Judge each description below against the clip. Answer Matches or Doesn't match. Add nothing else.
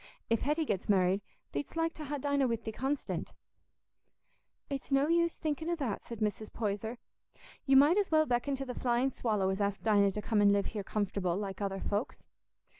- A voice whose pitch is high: Matches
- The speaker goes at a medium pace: Matches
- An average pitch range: Doesn't match